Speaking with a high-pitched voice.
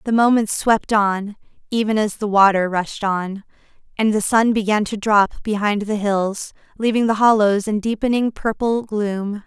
Yes: high, 210 Hz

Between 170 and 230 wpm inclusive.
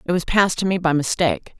No: fast, 265 wpm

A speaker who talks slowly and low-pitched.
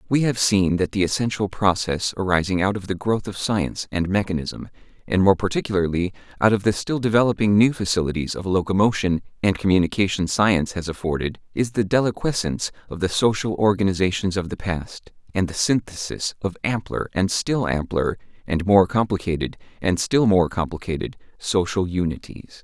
No: average, 160 wpm; very low, 95 Hz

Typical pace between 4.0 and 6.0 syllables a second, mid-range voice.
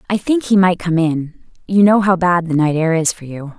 Yes: 5.1 syllables/s; medium, 175 Hz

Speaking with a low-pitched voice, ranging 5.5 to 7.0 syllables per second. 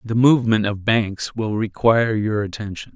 No: low, 110 Hz; 4.9 syllables/s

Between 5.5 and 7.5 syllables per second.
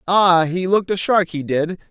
No: 4.9 syllables/s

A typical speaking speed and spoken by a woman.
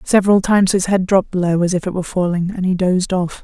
No: fast, 260 wpm; female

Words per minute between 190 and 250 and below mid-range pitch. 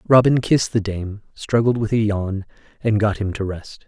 Yes: average, 200 wpm; low, 105 Hz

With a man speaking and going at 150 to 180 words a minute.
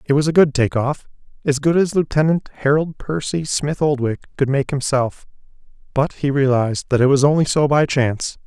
Yes: male; average, 175 wpm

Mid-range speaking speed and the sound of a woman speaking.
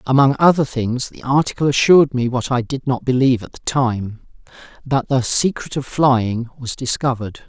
No: average, 175 wpm; male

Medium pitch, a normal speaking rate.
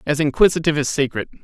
Yes: medium, 145 Hz; average, 170 wpm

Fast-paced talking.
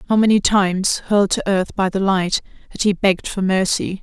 Yes: fast, 210 wpm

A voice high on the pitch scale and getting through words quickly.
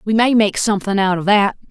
Yes: high, 205 Hz; fast, 245 wpm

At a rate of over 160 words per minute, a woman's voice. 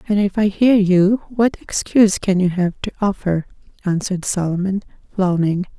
No: average, 155 wpm; female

